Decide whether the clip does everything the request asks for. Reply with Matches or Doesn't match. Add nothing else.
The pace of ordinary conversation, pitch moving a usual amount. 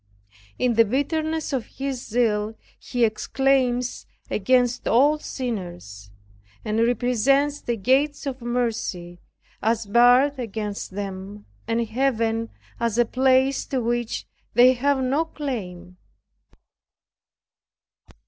Doesn't match